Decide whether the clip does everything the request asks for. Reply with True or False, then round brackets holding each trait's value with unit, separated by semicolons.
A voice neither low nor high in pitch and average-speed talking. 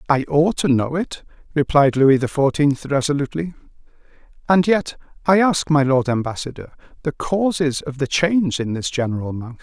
True (145 Hz; 160 wpm)